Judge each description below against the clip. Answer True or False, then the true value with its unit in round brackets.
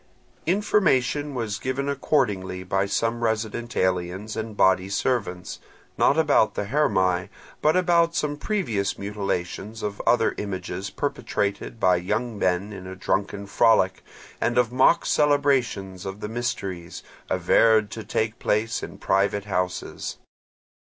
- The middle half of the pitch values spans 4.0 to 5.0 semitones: True (4.5 semitones)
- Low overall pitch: True (105 Hz)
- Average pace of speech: False (130 wpm)